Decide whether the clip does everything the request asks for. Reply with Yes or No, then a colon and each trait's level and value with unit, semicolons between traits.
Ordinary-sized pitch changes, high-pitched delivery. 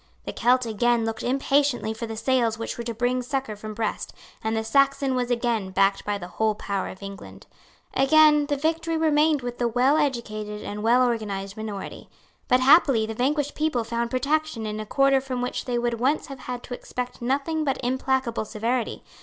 Yes: average, 3.7 semitones; high, 245 Hz